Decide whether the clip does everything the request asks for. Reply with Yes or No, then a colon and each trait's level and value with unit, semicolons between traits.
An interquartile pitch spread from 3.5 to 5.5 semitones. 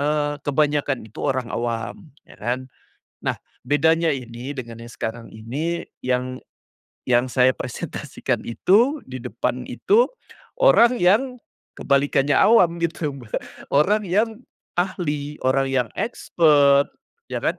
Yes: average, 5.2 semitones